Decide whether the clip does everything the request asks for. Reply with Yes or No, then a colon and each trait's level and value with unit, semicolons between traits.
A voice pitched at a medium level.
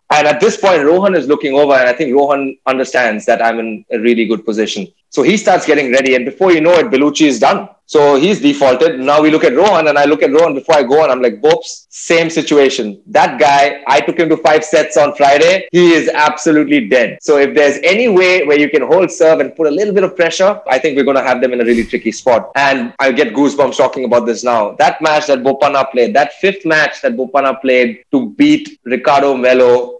Yes: medium, 145 Hz